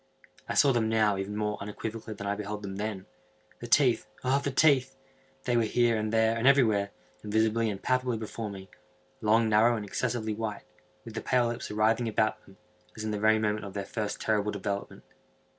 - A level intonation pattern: Yes, narrow, 2.1 semitones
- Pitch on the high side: No, low, 110 Hz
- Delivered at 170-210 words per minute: Yes, average, 190 wpm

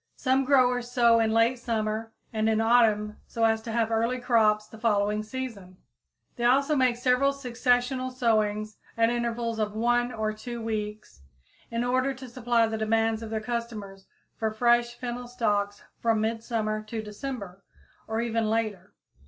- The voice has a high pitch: Yes, high, 230 Hz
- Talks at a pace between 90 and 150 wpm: No, average, 160 wpm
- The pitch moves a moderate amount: No, narrow, 2.0 semitones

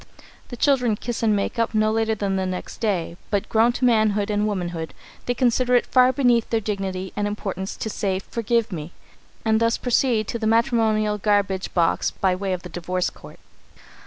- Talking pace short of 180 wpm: No, average, 190 wpm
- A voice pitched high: Yes, high, 215 Hz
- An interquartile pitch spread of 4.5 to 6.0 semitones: No, average, 3.3 semitones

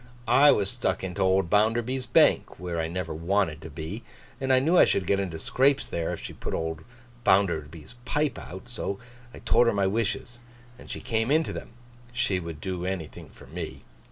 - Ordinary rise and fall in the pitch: No, wide, 6.0 semitones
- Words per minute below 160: No, average, 195 wpm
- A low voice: Yes, very low, 95 Hz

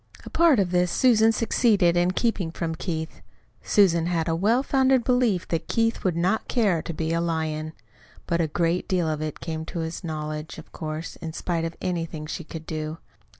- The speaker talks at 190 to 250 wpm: Yes, average, 195 wpm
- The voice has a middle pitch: Yes, medium, 170 Hz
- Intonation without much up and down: No, average, 3.7 semitones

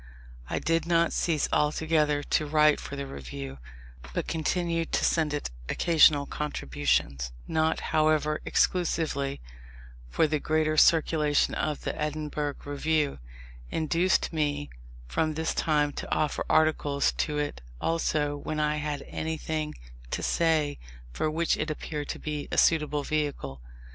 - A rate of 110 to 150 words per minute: Yes, slow, 135 wpm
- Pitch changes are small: Yes, narrow, 1.5 semitones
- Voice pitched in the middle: Yes, medium, 150 Hz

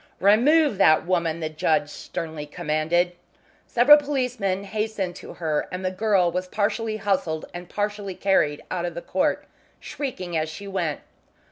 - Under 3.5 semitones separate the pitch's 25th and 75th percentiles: No, average, 4.4 semitones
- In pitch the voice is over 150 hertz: Yes, medium, 185 Hz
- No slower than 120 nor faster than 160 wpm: Yes, average, 145 wpm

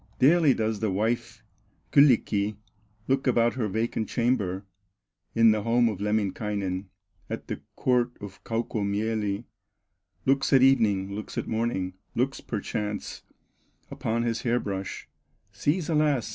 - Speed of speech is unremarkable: No, slow, 125 wpm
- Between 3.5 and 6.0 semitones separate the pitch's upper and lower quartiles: No, average, 3.1 semitones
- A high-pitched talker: No, low, 110 Hz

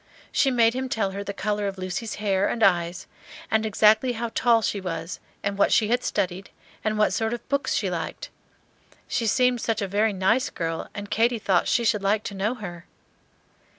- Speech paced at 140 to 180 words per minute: No, average, 200 wpm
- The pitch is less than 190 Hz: No, high, 210 Hz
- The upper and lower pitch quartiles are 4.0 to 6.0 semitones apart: No, average, 2.8 semitones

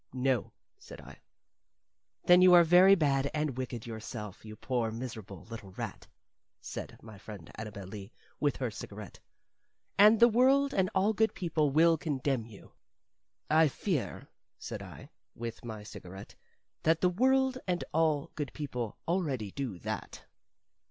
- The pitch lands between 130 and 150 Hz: Yes, medium, 140 Hz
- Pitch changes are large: Yes, wide, 8.2 semitones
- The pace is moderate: Yes, average, 145 wpm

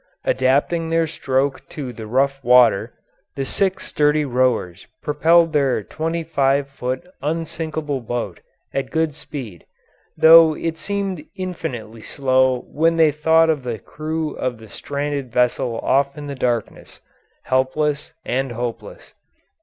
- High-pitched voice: No, medium, 140 Hz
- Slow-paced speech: Yes, slow, 130 wpm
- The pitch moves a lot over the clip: No, average, 4.1 semitones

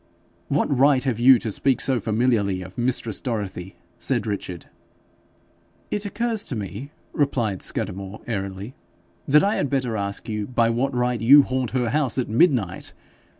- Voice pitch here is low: Yes, low, 120 Hz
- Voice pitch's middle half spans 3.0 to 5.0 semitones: Yes, average, 4.6 semitones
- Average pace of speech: Yes, average, 155 wpm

